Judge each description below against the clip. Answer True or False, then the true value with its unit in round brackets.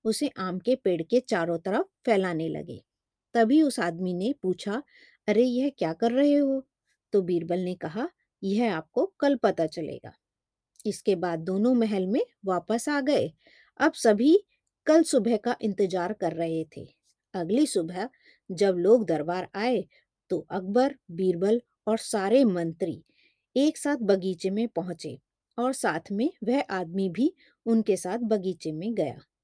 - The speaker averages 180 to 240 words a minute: False (150 wpm)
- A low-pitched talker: False (215 Hz)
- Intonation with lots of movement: True (6.0 semitones)